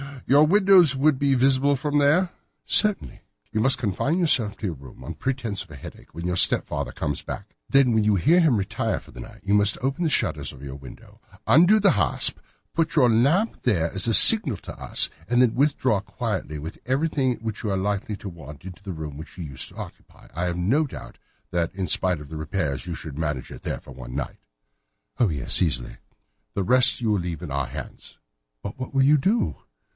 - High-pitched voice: No, low, 110 Hz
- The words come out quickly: Yes, fast, 215 wpm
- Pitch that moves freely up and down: Yes, wide, 8.1 semitones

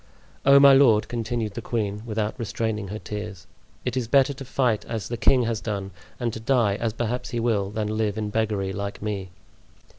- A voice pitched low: Yes, low, 110 Hz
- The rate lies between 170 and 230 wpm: Yes, average, 200 wpm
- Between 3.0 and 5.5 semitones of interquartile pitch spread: No, narrow, 2.4 semitones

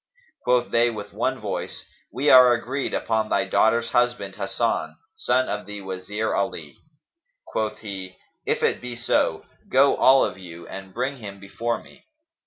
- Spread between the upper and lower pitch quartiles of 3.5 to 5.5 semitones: Yes, average, 3.9 semitones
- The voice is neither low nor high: No, low, 110 Hz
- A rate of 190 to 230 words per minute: No, average, 160 wpm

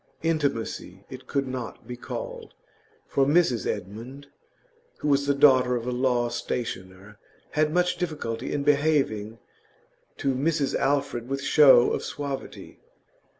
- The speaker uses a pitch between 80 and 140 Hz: Yes, low, 135 Hz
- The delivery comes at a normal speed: No, slow, 130 wpm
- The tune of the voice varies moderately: Yes, average, 3.4 semitones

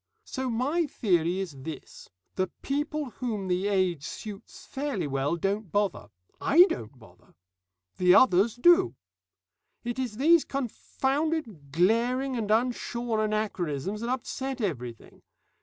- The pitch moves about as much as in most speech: No, wide, 6.6 semitones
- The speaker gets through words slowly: Yes, slow, 125 wpm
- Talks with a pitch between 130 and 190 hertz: No, high, 215 Hz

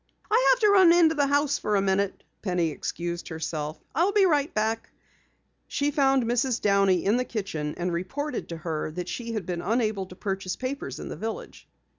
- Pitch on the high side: Yes, high, 215 Hz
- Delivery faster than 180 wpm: Yes, average, 190 wpm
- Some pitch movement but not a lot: No, wide, 7.8 semitones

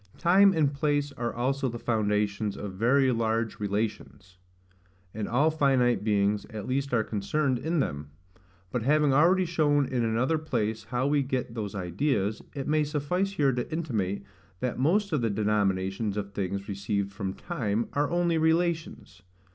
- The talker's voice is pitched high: No, low, 125 Hz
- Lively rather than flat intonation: Yes, wide, 6.1 semitones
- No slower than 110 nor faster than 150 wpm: No, average, 160 wpm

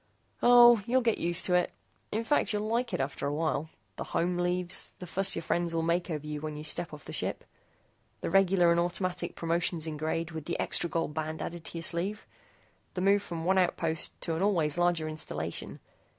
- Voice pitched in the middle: Yes, medium, 170 Hz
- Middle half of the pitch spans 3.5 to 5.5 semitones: No, average, 2.7 semitones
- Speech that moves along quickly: Yes, fast, 210 wpm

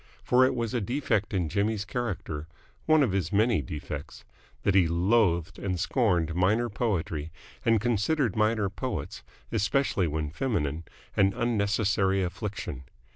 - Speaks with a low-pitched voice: Yes, low, 100 Hz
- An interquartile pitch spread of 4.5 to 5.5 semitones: Yes, average, 5.1 semitones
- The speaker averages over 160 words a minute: No, slow, 135 wpm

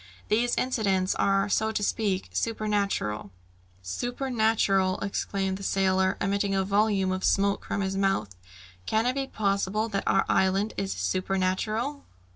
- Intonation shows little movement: Yes, narrow, 2.3 semitones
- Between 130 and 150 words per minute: Yes, average, 140 wpm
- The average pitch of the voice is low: No, high, 195 Hz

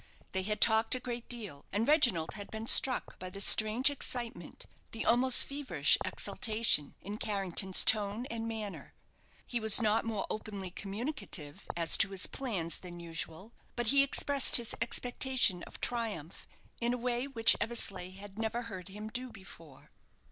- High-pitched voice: Yes, high, 220 Hz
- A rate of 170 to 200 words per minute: No, average, 160 wpm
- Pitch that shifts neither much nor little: Yes, average, 4.0 semitones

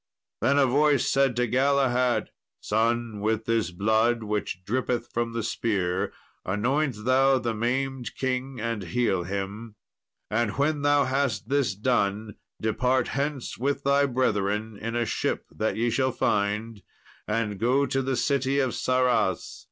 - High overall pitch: No, low, 120 Hz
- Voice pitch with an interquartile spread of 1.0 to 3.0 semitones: No, average, 3.7 semitones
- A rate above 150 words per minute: No, average, 145 wpm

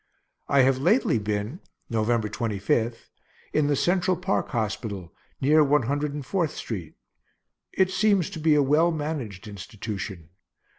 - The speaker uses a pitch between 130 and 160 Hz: Yes, low, 135 Hz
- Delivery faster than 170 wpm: No, average, 140 wpm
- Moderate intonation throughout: No, wide, 6.4 semitones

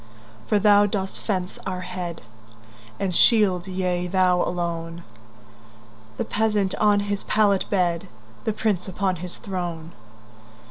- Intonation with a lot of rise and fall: Yes, wide, 9.0 semitones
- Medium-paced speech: No, slow, 100 wpm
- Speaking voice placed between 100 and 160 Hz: No, medium, 180 Hz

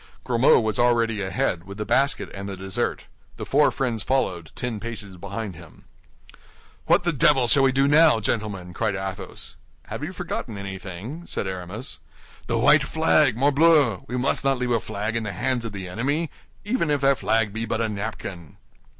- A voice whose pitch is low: Yes, low, 115 Hz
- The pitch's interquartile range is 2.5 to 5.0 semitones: No, wide, 5.5 semitones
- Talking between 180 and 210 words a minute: Yes, average, 185 wpm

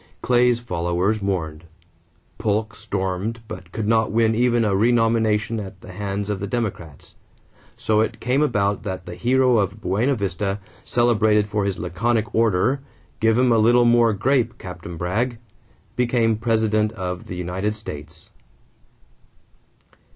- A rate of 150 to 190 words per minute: No, average, 140 wpm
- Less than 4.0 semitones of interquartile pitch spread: Yes, average, 3.6 semitones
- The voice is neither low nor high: No, low, 105 Hz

